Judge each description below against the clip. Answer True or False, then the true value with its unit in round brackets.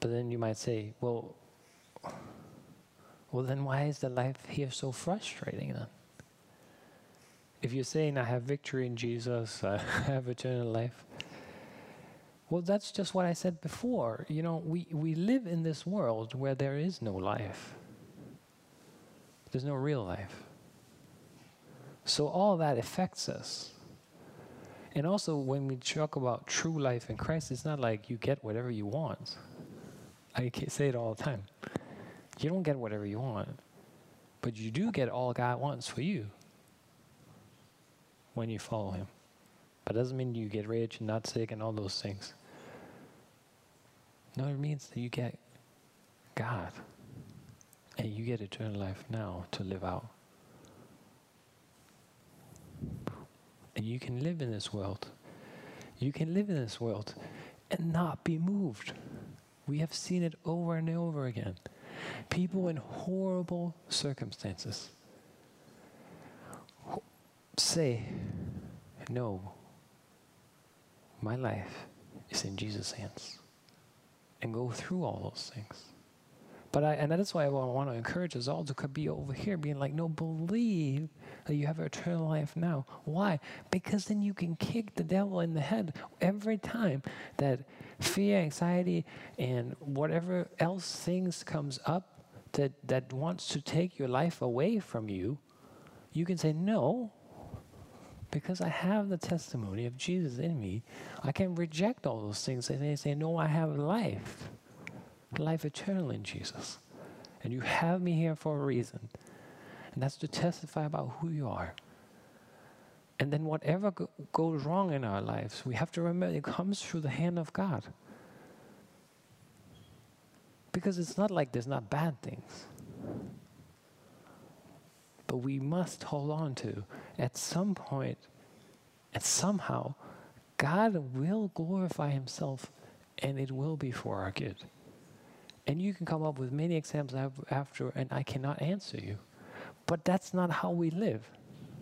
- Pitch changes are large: True (5.7 semitones)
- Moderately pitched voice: True (145 Hz)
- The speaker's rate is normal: True (145 wpm)